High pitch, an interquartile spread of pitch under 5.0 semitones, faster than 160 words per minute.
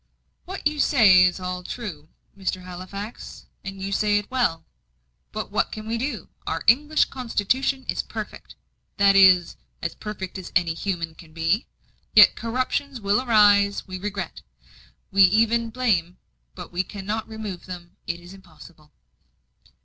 No: high, 200 Hz; average, 3.9 semitones; average, 150 wpm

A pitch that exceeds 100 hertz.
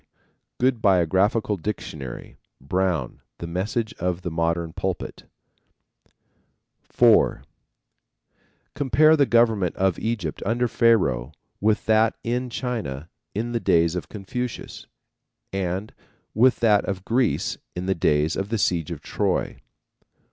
No: very low, 95 Hz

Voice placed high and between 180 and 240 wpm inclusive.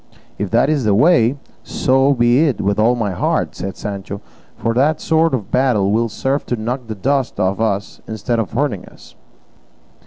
No: low, 115 Hz; average, 185 wpm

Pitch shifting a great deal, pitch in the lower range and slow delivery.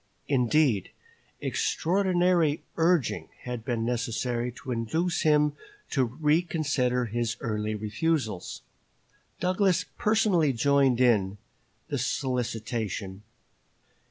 Yes: wide, 5.9 semitones; low, 130 Hz; slow, 85 wpm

